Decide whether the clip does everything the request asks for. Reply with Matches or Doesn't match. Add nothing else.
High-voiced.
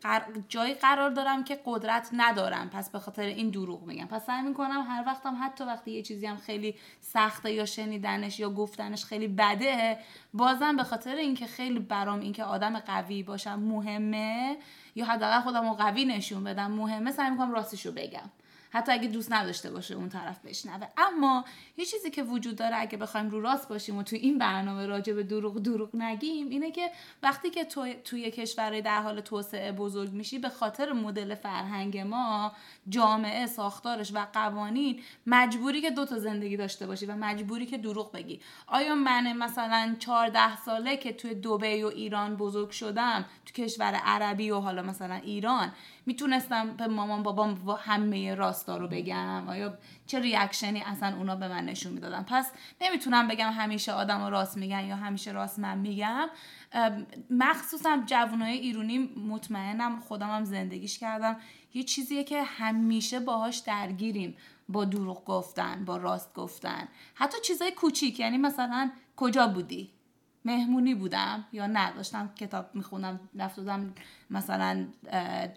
Matches